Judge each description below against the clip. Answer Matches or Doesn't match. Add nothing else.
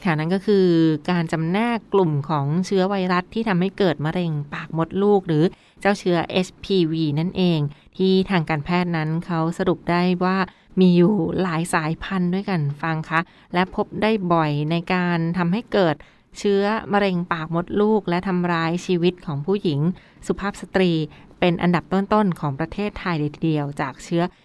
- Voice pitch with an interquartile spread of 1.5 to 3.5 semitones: Matches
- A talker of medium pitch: Matches